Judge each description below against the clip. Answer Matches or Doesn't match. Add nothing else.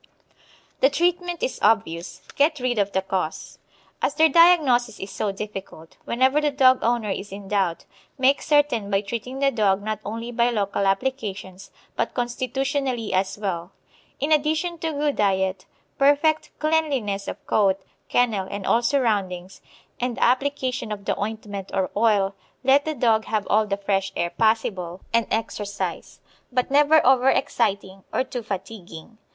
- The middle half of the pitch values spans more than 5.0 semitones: Matches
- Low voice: Doesn't match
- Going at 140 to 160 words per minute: Matches